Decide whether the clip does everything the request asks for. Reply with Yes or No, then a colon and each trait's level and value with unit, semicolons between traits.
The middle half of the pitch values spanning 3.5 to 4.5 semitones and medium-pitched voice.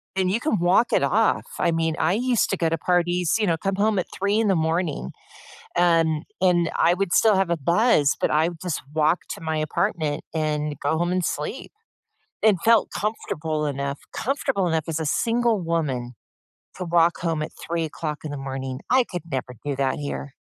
Yes: average, 3.8 semitones; medium, 170 Hz